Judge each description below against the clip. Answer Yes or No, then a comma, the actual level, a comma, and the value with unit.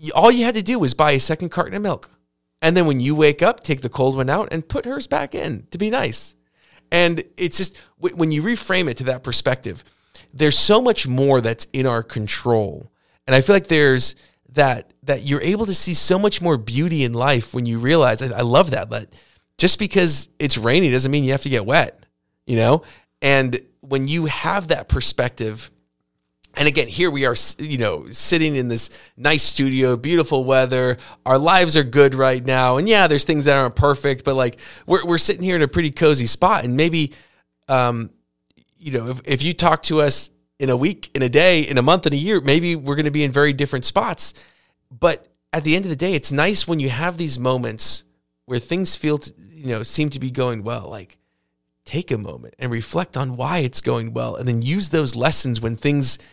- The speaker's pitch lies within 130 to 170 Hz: Yes, medium, 140 Hz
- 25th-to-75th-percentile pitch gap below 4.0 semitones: No, average, 4.6 semitones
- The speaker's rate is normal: No, fast, 215 wpm